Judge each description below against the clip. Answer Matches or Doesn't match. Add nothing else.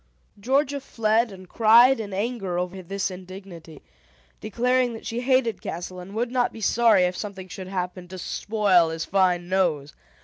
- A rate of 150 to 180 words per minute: Matches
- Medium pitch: Doesn't match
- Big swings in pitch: Doesn't match